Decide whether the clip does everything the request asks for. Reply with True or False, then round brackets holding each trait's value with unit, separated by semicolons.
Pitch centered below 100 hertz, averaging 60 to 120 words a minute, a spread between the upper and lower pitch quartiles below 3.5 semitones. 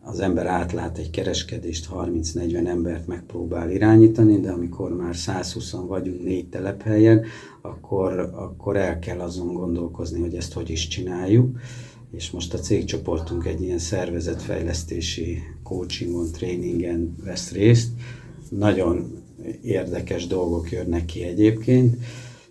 False (90 Hz; 115 wpm; 3.8 semitones)